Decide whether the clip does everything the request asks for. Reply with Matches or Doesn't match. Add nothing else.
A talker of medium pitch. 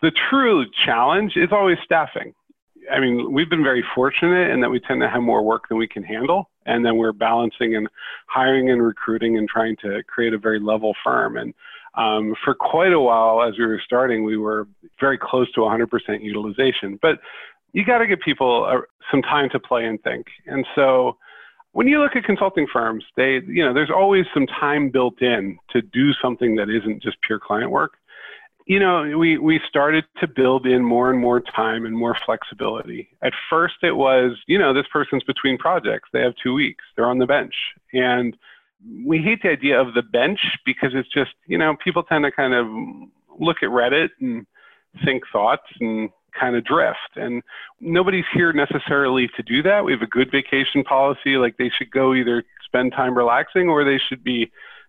Doesn't match